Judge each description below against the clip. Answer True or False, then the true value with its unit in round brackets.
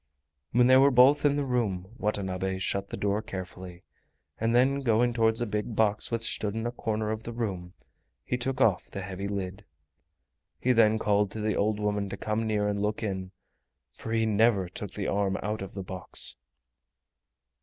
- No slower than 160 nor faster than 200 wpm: True (190 wpm)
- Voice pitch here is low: True (105 Hz)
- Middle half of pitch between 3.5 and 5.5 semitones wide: False (2.7 semitones)